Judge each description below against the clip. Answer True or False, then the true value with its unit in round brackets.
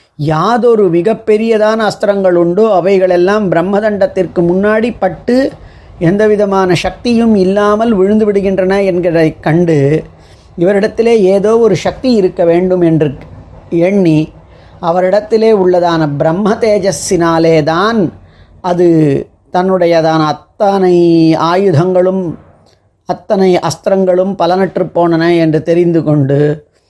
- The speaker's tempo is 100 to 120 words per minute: False (85 wpm)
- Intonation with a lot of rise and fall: False (3.7 semitones)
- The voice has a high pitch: False (180 Hz)